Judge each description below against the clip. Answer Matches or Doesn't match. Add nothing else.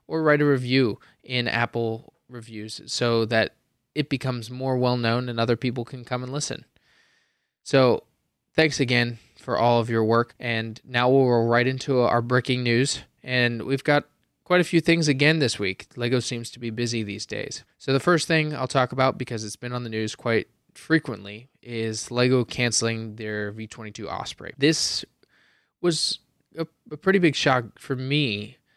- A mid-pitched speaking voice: Doesn't match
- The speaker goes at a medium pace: Matches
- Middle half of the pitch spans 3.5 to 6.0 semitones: Doesn't match